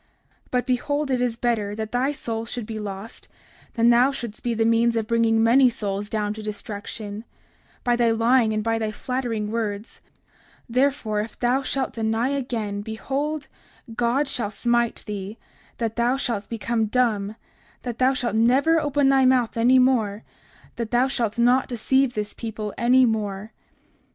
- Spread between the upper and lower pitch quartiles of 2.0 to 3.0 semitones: Yes, average, 2.7 semitones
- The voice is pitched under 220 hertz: No, high, 230 Hz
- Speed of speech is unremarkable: Yes, average, 170 wpm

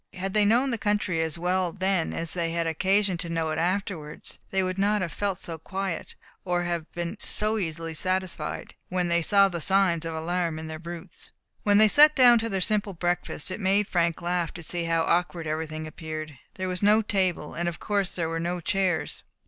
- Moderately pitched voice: Yes, medium, 180 Hz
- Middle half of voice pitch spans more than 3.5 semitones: No, average, 2.9 semitones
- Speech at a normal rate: No, fast, 210 wpm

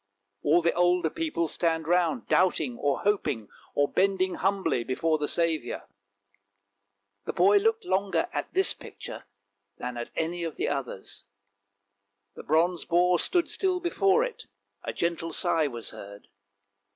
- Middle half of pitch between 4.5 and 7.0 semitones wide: Yes, average, 4.8 semitones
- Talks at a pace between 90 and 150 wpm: Yes, average, 145 wpm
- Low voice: No, medium, 170 Hz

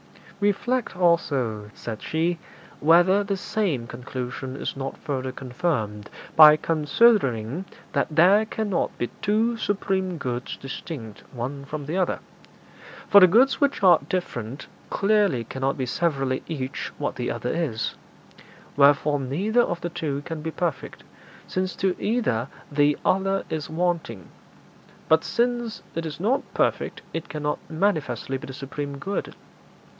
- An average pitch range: No, wide, 6.2 semitones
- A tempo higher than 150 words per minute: No, average, 140 wpm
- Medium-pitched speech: Yes, medium, 160 Hz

